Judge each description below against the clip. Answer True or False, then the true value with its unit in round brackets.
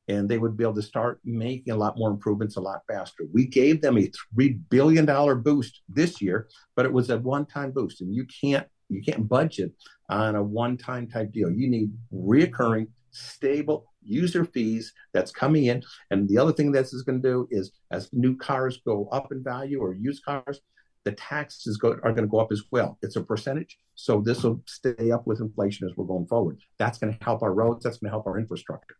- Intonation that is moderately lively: True (3.6 semitones)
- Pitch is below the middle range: True (120 Hz)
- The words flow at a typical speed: False (225 wpm)